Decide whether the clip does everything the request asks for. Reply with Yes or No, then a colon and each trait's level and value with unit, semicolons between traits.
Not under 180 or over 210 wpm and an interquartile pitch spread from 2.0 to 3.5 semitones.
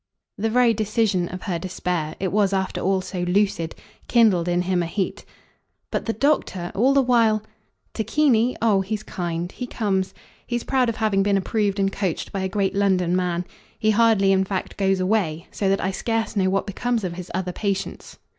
Yes: average, 195 wpm; average, 3.1 semitones